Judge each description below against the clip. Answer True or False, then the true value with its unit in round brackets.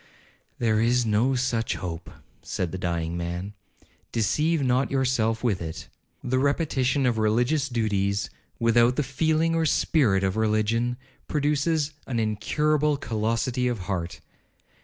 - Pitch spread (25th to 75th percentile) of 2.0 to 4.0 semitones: False (4.7 semitones)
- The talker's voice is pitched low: True (120 Hz)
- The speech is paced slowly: True (130 wpm)